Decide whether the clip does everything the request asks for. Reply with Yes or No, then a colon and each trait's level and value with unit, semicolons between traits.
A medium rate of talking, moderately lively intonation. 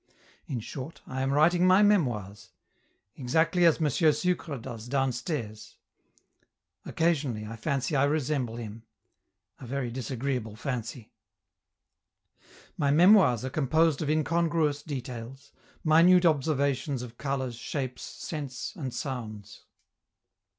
No: slow, 110 wpm; average, 4.4 semitones